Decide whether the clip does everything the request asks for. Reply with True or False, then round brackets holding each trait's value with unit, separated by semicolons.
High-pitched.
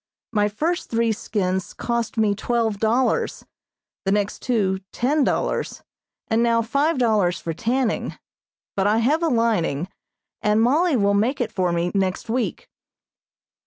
True (225 Hz)